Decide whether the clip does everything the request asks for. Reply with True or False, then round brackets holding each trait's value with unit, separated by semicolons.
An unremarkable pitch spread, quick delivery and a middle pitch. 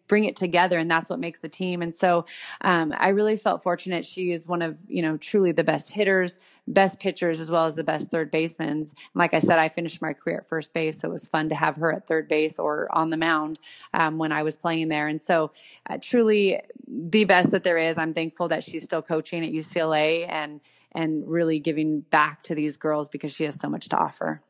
False (2.0 semitones; 240 wpm; 165 Hz)